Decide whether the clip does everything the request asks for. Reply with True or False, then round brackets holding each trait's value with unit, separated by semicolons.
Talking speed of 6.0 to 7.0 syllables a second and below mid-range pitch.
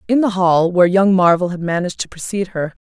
False (6.5 syllables/s; 185 Hz)